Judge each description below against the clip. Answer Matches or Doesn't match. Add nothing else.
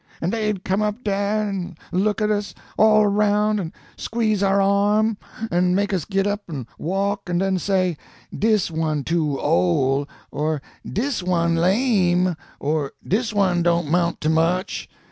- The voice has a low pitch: Doesn't match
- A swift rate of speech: Doesn't match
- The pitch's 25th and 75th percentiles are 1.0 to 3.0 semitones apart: Doesn't match